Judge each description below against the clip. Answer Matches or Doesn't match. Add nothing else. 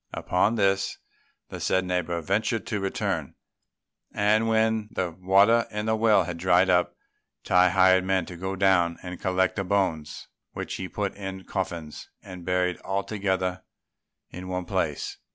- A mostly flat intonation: Matches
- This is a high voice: Doesn't match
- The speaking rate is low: Doesn't match